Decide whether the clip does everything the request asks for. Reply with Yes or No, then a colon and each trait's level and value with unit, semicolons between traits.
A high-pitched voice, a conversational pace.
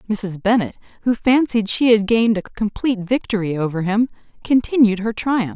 Yes: high, 215 Hz; average, 160 wpm